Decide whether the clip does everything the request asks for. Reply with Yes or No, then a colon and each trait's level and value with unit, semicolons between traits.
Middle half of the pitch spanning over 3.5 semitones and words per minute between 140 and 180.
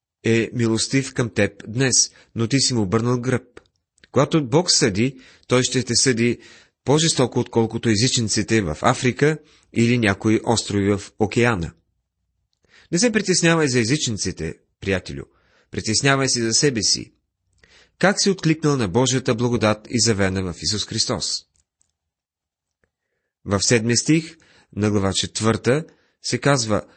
No: average, 4.5 semitones; average, 130 wpm